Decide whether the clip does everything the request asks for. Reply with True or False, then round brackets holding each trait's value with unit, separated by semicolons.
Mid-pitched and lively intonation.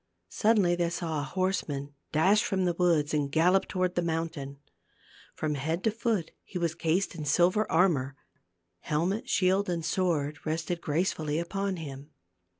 False (170 Hz; 3.5 semitones)